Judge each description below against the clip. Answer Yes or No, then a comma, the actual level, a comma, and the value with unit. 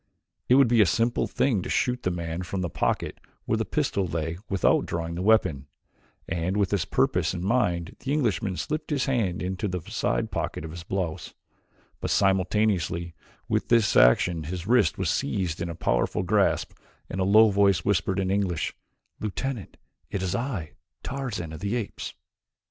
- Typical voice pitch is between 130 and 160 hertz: No, very low, 95 Hz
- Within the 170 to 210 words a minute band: Yes, average, 175 wpm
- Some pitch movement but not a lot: Yes, average, 4.3 semitones